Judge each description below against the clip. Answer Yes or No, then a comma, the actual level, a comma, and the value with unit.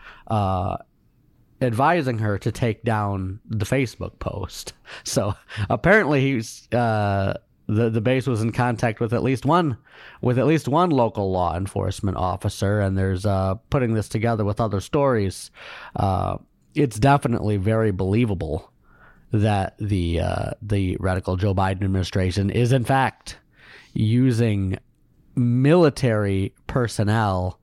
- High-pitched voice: No, low, 110 Hz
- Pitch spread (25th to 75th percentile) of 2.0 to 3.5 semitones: No, average, 4.2 semitones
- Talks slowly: Yes, slow, 130 wpm